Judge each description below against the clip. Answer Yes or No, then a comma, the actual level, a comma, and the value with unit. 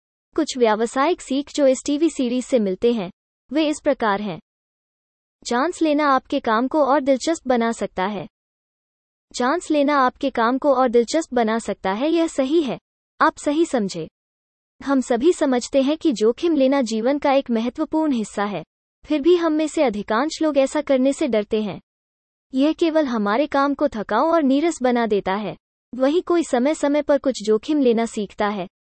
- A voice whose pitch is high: Yes, very high, 270 Hz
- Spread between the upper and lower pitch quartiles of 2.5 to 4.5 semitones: No, average, 5.1 semitones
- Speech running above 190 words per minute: No, average, 180 wpm